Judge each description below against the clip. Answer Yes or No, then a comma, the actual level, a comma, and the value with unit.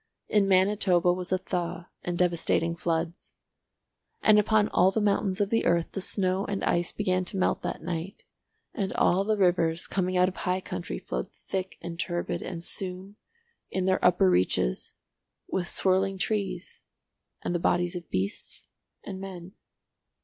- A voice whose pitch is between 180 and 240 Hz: Yes, medium, 185 Hz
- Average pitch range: No, narrow, 2.0 semitones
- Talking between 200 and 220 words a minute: No, average, 155 wpm